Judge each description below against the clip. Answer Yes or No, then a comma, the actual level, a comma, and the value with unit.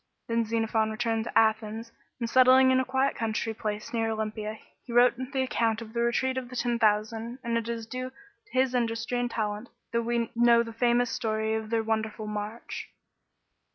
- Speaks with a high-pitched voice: Yes, high, 230 Hz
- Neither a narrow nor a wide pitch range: No, narrow, 1.8 semitones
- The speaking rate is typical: Yes, average, 190 wpm